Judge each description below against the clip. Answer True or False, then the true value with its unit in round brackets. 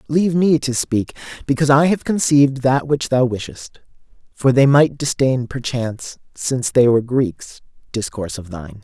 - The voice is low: True (130 Hz)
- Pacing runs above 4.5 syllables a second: True (5.2 syllables/s)